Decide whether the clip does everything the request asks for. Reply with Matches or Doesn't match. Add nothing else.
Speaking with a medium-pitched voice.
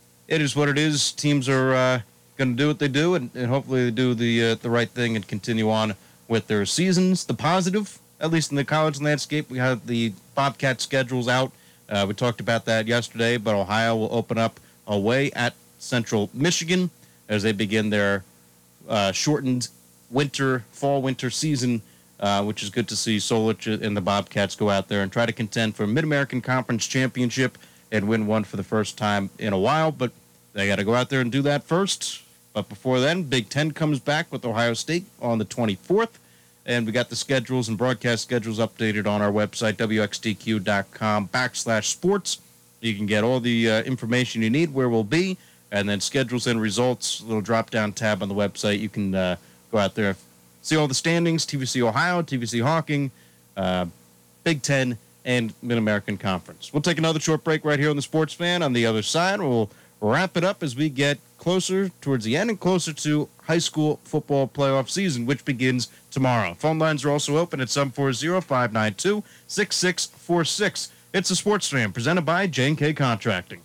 Doesn't match